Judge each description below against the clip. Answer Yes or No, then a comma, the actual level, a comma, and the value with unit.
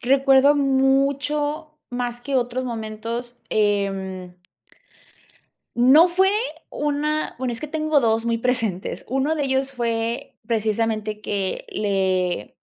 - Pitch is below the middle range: No, high, 245 Hz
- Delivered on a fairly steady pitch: No, average, 4.3 semitones